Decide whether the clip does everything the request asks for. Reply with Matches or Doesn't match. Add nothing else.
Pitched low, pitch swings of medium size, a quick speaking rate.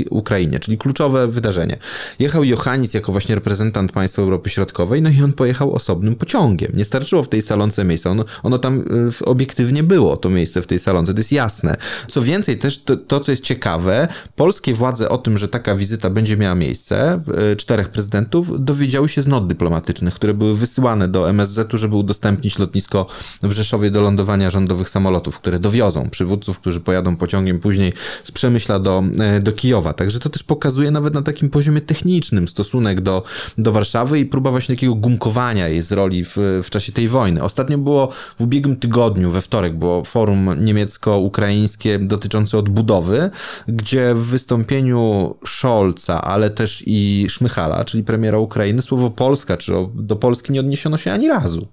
Matches